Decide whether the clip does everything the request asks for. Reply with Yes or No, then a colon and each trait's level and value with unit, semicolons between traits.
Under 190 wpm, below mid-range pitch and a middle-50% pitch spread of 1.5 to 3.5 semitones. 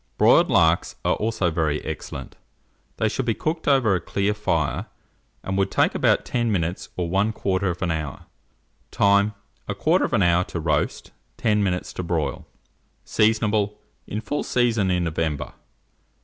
No: average, 140 wpm; very low, 95 Hz; average, 4.3 semitones